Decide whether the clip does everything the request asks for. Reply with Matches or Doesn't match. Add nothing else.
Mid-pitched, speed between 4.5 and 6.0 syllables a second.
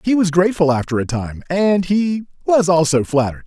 Matches